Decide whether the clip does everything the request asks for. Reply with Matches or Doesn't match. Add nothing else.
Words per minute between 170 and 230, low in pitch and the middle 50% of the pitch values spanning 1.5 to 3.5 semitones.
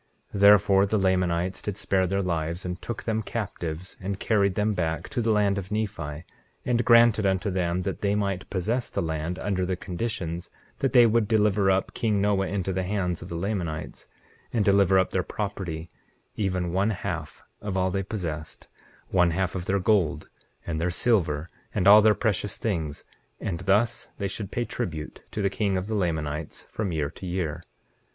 Matches